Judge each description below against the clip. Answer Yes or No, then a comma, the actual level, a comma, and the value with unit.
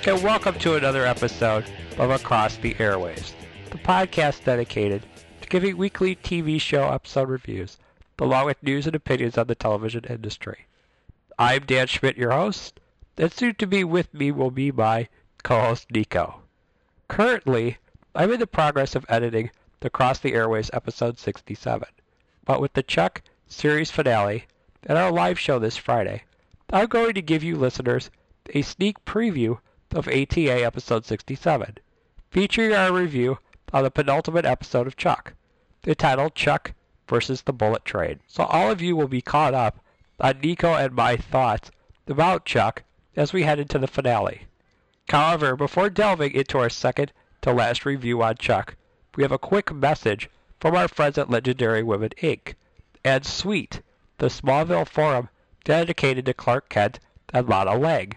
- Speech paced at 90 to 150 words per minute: No, average, 160 wpm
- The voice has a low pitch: Yes, low, 130 Hz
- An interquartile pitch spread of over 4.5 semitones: Yes, average, 5.2 semitones